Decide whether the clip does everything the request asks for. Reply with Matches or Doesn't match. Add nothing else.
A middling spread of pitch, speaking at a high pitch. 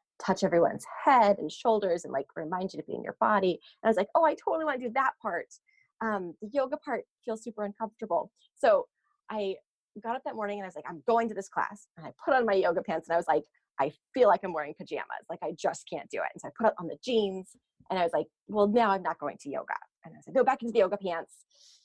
Doesn't match